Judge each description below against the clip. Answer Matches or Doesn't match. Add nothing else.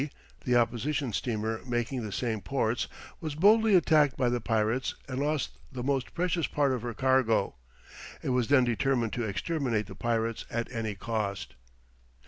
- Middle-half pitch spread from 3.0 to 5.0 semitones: Matches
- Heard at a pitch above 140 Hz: Doesn't match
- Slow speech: Doesn't match